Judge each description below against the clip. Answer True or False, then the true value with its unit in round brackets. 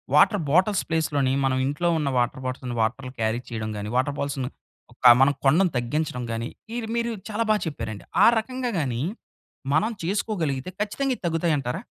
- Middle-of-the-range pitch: True (145 Hz)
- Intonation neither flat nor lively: False (7.0 semitones)